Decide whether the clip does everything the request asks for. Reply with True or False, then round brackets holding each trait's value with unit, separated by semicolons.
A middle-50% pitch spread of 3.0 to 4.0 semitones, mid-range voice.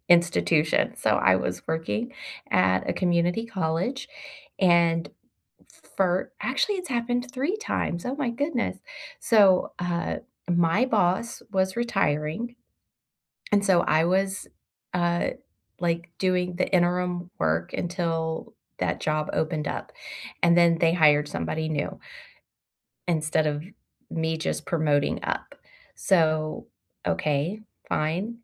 True (3.4 semitones; 175 Hz)